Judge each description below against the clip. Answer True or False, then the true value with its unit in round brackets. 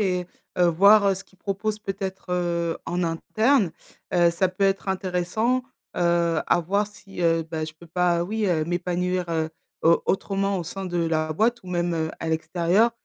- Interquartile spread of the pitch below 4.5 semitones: True (2.6 semitones)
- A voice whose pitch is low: False (180 Hz)